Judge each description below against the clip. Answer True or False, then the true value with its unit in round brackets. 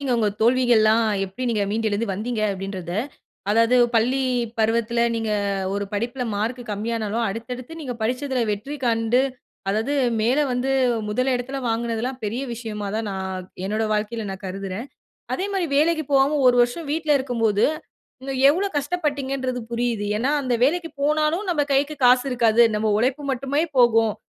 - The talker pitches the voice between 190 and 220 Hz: False (240 Hz)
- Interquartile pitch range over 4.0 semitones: False (3.7 semitones)